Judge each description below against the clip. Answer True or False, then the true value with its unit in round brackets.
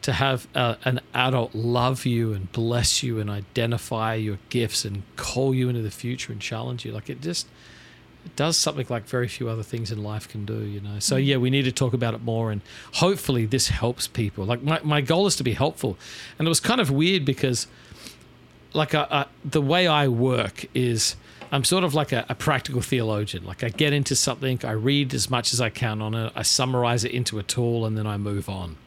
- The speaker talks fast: True (230 wpm)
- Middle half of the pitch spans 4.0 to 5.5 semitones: False (3.6 semitones)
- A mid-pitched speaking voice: False (125 Hz)